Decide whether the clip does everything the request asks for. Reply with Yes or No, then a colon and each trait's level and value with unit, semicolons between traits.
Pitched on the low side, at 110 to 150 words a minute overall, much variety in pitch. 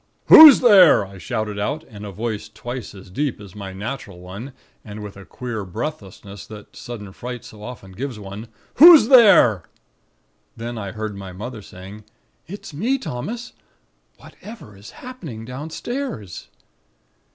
Yes: low, 110 Hz; average, 145 wpm; wide, 6.6 semitones